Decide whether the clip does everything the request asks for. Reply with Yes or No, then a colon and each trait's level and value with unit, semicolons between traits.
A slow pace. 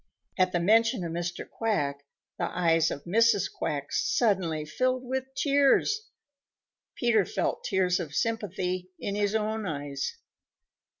Yes: slow, 130 wpm